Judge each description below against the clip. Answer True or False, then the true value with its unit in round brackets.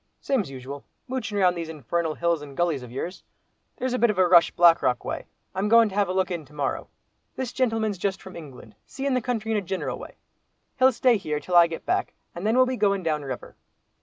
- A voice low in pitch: False (185 Hz)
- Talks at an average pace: False (235 wpm)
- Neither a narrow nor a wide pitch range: False (5.9 semitones)